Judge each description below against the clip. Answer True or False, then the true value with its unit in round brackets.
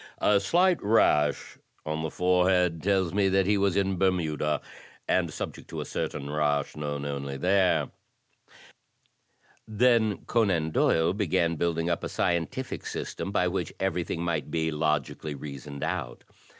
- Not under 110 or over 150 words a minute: True (140 wpm)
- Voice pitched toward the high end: False (85 Hz)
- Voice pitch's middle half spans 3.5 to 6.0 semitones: True (4.2 semitones)